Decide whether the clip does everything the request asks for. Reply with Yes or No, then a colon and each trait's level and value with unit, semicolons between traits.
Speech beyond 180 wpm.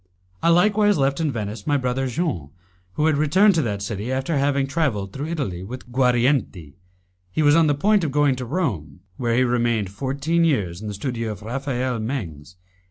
Yes: average, 190 wpm